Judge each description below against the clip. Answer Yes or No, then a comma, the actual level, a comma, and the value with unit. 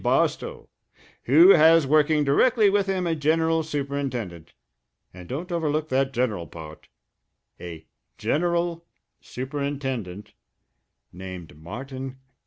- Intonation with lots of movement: Yes, wide, 6.9 semitones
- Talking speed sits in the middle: No, slow, 105 wpm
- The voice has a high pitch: No, medium, 140 Hz